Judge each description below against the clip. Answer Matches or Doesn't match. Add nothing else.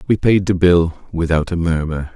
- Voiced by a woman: Doesn't match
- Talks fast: Doesn't match